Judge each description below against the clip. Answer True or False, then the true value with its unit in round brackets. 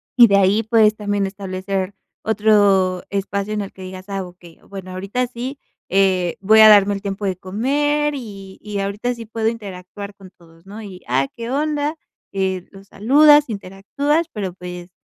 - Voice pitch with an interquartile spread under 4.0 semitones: True (3.0 semitones)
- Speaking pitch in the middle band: False (200 Hz)